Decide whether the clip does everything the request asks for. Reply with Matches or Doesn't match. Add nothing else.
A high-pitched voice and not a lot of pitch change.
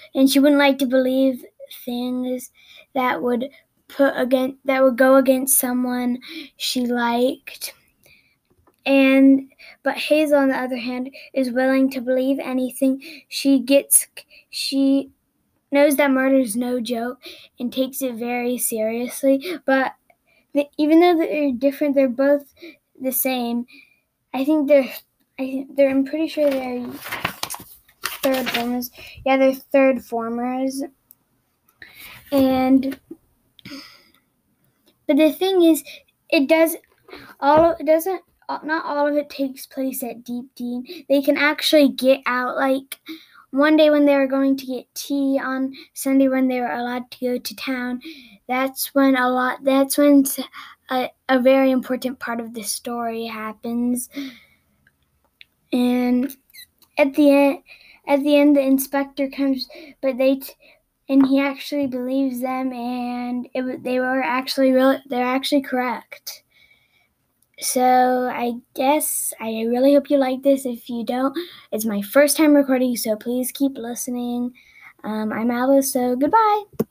Matches